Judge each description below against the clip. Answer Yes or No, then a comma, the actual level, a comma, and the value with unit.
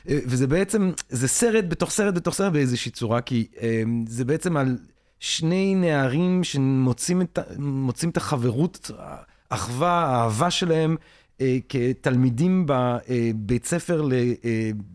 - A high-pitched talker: No, low, 135 Hz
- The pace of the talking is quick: No, average, 125 wpm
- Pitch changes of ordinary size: No, wide, 6.0 semitones